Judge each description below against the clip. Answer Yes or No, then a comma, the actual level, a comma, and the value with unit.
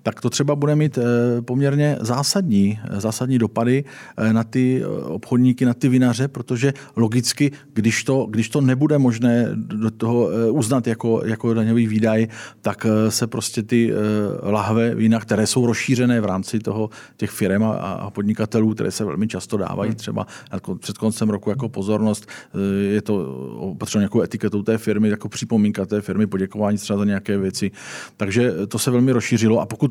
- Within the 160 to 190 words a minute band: Yes, average, 165 wpm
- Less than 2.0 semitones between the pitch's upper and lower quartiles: No, average, 2.7 semitones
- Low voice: Yes, low, 115 Hz